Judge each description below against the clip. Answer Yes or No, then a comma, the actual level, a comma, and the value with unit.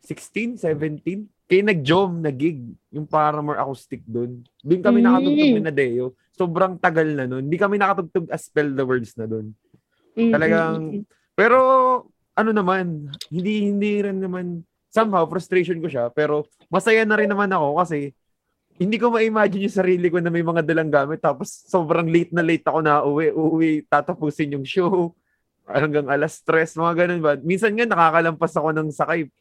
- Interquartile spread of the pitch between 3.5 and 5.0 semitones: Yes, average, 4.5 semitones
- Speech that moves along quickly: Yes, fast, 165 wpm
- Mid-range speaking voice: Yes, medium, 170 Hz